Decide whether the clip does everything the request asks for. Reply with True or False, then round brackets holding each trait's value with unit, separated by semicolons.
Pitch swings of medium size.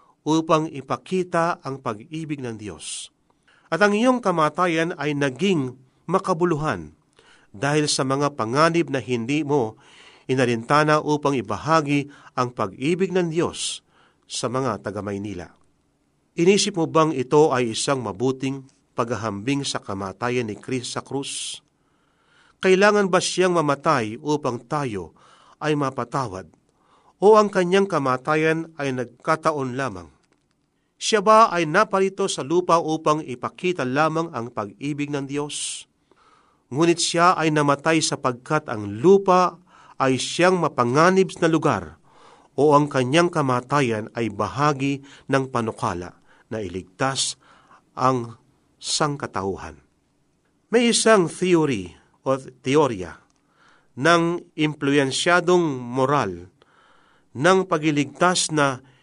True (4.9 semitones)